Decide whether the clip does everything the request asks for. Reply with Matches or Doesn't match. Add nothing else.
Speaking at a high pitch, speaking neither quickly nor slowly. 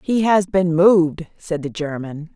Doesn't match